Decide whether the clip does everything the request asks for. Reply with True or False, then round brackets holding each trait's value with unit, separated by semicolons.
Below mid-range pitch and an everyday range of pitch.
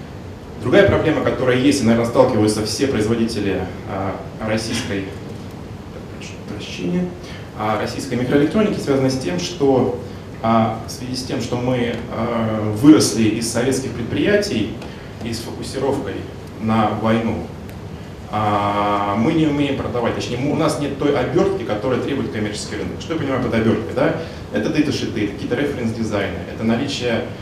True (110 Hz; 3.6 semitones)